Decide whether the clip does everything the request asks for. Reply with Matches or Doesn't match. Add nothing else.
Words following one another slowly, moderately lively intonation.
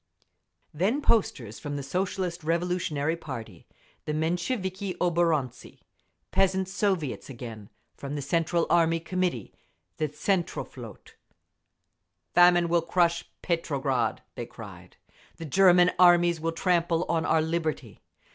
Matches